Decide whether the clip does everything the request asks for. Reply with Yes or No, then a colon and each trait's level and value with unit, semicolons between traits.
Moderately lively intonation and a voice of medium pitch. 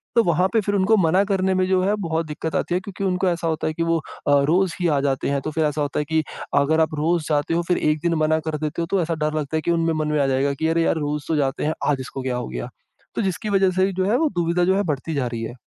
Yes: average, 3.6 semitones; medium, 160 Hz